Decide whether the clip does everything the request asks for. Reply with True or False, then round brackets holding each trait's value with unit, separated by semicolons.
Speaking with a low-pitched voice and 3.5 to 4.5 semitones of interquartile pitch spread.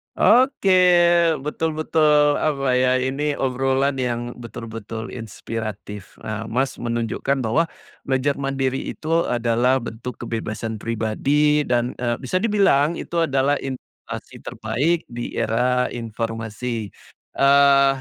True (130 Hz; 4.1 semitones)